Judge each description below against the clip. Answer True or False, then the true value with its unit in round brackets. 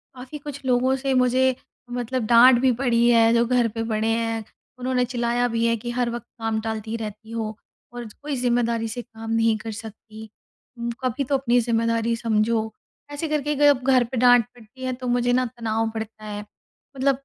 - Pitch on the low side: False (235 Hz)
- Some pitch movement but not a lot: False (2.1 semitones)